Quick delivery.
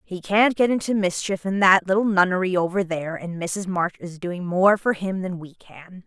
Yes: fast, 220 wpm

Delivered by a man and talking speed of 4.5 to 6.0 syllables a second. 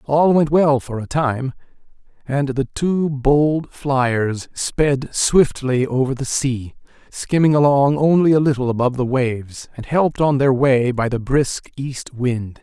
No: male; 3.9 syllables/s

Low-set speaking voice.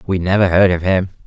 Yes: very low, 95 Hz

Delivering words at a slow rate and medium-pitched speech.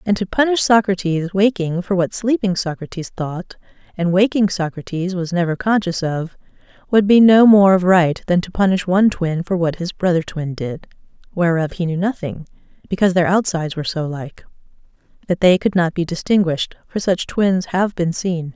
No: average, 180 wpm; medium, 180 Hz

